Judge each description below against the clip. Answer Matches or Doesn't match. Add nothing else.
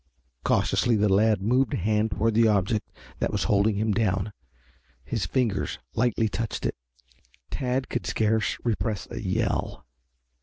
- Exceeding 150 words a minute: Doesn't match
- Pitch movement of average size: Doesn't match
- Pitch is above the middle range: Doesn't match